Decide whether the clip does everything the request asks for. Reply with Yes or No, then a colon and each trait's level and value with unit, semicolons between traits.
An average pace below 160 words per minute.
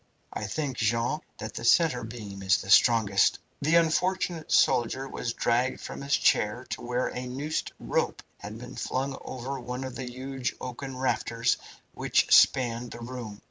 No: average, 165 wpm